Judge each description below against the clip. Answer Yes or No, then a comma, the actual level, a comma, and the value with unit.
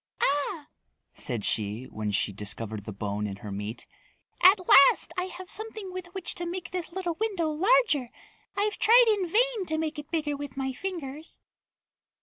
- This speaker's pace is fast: No, average, 170 wpm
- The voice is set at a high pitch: Yes, very high, 315 Hz